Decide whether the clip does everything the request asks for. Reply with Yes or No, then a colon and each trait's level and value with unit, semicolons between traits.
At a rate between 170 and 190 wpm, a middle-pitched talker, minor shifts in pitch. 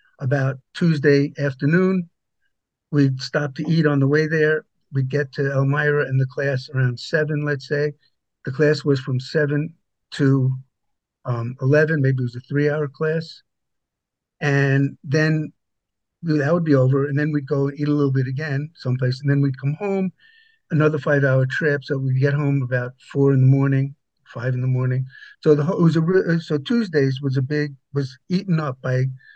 Yes: average, 175 wpm; medium, 145 Hz; narrow, 2.3 semitones